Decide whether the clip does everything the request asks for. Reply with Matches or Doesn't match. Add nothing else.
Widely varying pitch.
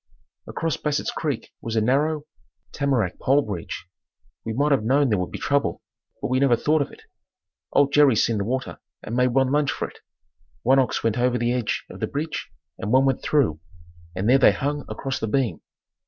Doesn't match